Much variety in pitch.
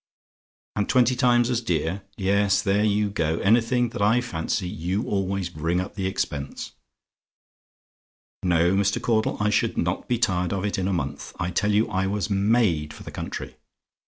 No: average, 3.5 semitones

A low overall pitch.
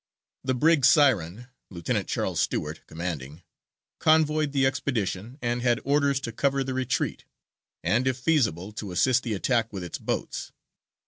Yes: low, 125 Hz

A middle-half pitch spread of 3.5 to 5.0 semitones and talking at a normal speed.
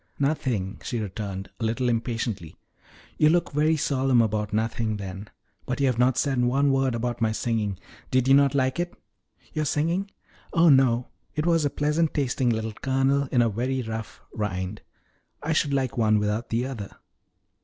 Yes: average, 4.1 semitones; average, 175 wpm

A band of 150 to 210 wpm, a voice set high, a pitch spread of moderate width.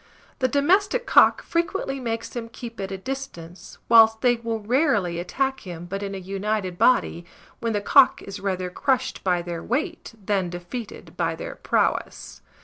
No: average, 165 wpm; high, 225 Hz; wide, 5.7 semitones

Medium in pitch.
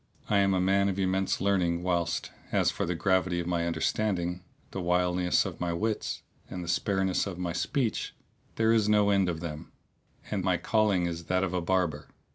No: very low, 90 Hz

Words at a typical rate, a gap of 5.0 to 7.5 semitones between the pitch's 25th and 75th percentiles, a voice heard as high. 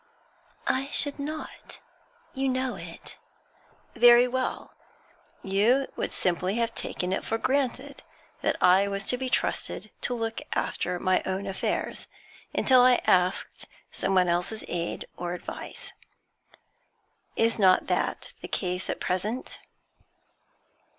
No: slow, 125 wpm; wide, 5.6 semitones; high, 220 Hz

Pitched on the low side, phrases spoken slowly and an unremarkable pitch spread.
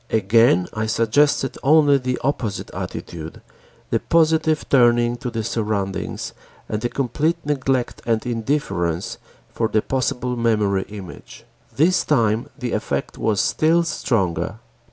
Yes: low, 120 Hz; slow, 125 wpm; average, 4.6 semitones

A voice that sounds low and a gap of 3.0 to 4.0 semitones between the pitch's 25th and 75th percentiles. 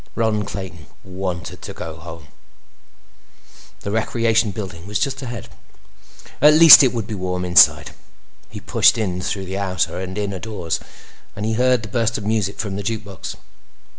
Yes: low, 100 Hz; average, 3.4 semitones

